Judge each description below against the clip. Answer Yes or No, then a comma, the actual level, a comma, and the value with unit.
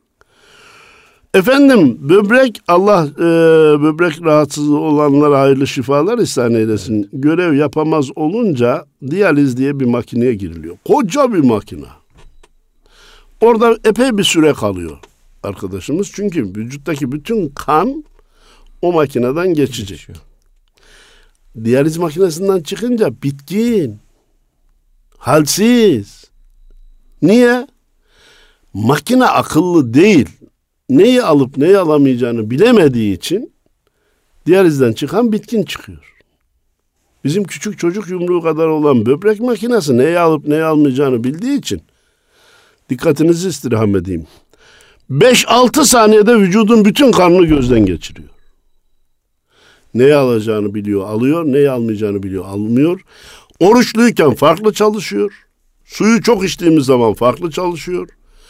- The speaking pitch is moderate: Yes, medium, 155 Hz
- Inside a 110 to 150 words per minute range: No, average, 100 wpm